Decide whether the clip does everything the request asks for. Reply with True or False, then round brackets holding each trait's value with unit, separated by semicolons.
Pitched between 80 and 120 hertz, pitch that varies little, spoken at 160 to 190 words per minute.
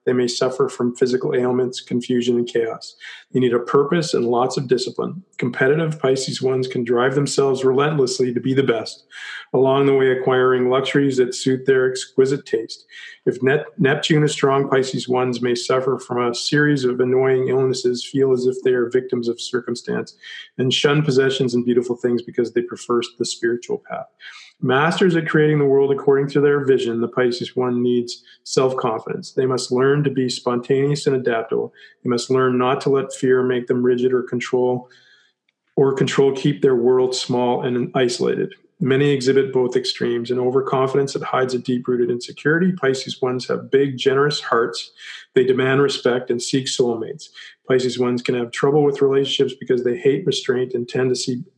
False (130 Hz; 2.0 semitones; 175 wpm)